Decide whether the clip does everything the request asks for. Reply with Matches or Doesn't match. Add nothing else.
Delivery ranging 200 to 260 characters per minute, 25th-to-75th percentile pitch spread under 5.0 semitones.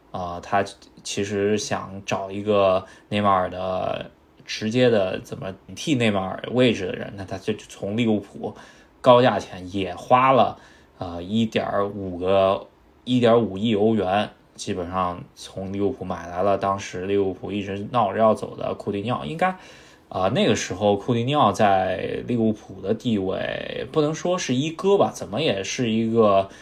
Matches